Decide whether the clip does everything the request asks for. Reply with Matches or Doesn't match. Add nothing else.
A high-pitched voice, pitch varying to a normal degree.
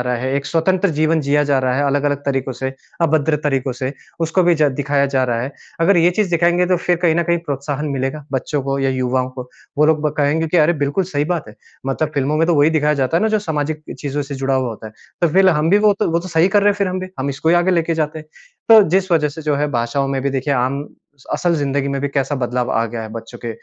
Doesn't match